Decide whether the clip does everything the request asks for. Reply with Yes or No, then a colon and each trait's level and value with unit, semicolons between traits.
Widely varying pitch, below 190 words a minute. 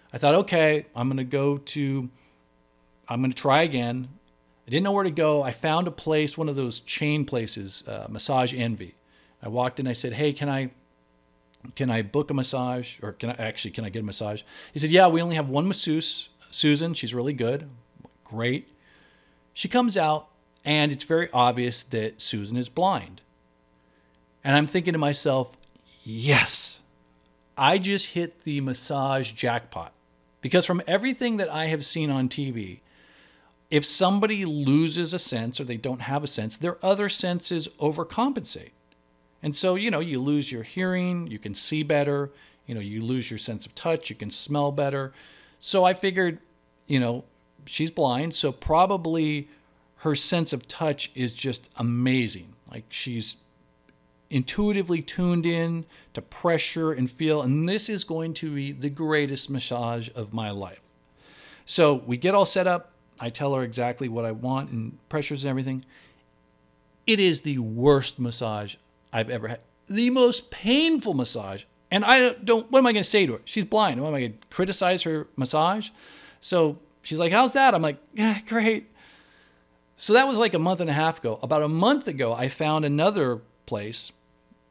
Yes: wide, 6.5 semitones; average, 175 wpm